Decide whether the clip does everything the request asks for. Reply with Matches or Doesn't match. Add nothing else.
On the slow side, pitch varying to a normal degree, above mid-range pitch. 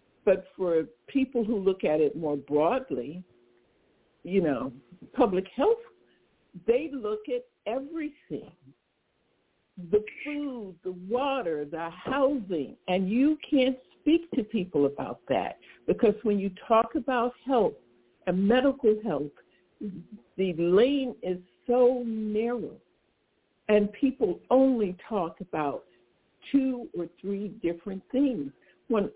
Doesn't match